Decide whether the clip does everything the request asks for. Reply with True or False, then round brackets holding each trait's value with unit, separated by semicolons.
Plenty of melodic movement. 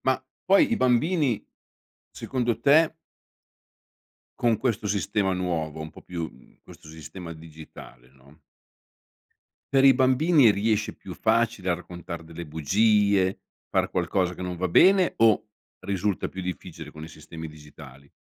True (6.5 semitones)